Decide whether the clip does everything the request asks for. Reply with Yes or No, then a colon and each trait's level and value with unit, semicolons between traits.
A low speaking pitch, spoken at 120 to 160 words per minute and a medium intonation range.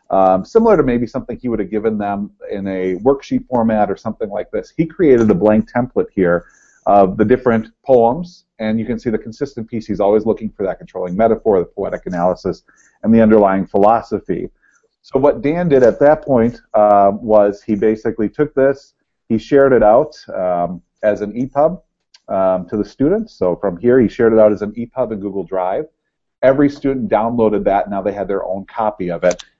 No: low, 110 Hz; fast, 205 wpm; average, 4.5 semitones